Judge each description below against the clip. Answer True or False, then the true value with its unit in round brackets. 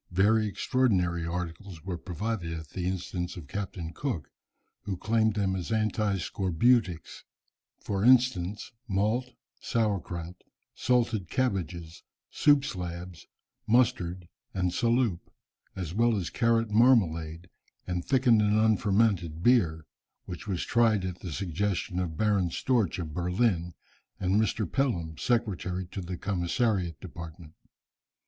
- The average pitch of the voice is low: True (95 Hz)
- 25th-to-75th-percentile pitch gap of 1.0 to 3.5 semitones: False (4.3 semitones)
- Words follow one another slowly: True (125 wpm)